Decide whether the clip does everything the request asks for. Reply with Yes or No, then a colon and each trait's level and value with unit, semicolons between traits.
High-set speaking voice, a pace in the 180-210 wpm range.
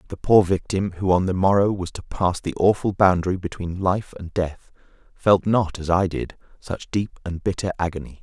No: very low, 90 Hz; average, 195 wpm